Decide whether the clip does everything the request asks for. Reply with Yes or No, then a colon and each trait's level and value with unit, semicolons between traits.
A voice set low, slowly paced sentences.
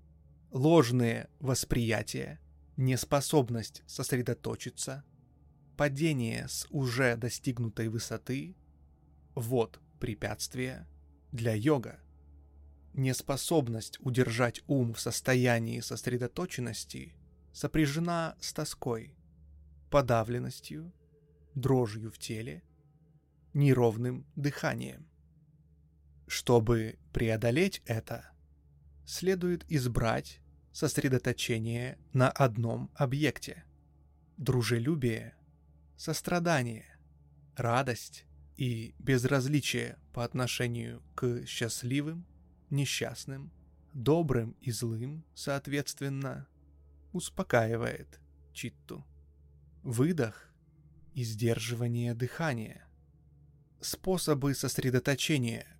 Yes: low, 120 Hz; slow, 60 wpm